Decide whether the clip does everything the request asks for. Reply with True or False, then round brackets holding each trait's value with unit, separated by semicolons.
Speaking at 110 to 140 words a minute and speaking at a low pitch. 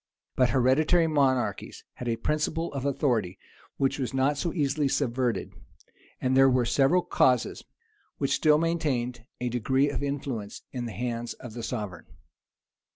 False (150 wpm; 130 Hz)